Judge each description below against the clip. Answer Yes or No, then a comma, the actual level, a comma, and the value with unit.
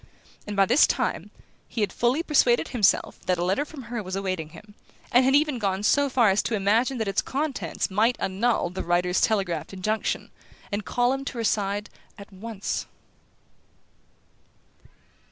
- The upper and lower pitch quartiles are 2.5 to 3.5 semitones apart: No, average, 4.2 semitones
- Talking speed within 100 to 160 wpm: No, average, 170 wpm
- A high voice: Yes, high, 210 Hz